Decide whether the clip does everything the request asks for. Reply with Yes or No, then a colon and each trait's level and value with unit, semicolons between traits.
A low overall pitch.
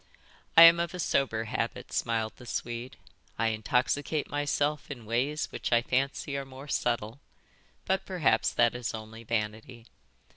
Yes: low, 125 Hz